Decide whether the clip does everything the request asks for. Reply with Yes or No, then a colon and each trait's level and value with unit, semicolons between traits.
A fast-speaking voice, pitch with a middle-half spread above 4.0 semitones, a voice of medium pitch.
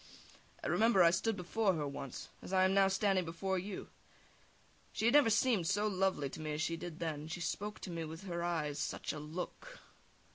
No: fast, 220 wpm; average, 3.4 semitones; medium, 180 Hz